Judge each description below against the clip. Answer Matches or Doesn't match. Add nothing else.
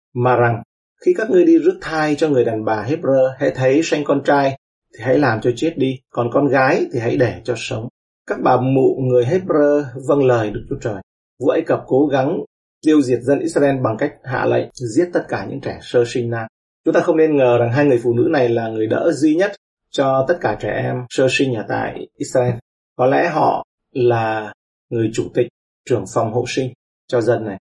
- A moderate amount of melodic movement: Matches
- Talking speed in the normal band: Matches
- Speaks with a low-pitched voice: Matches